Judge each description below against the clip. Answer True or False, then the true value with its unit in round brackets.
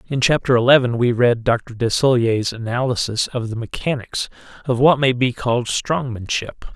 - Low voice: True (120 Hz)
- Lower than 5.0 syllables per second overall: False (5.1 syllables/s)